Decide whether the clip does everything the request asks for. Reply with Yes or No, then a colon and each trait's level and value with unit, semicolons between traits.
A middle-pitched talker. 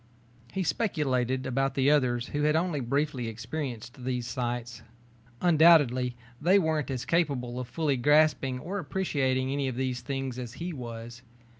No: low, 130 Hz